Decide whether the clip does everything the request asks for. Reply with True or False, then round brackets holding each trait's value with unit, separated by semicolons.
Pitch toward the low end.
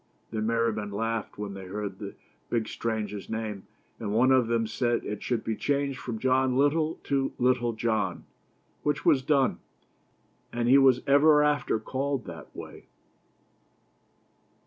True (120 Hz)